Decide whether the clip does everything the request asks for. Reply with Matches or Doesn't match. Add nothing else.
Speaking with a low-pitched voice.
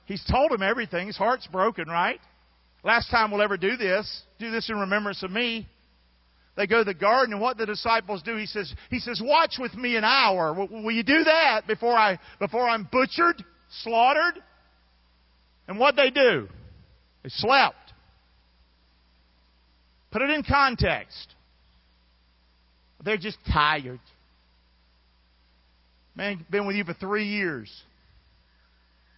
Doesn't match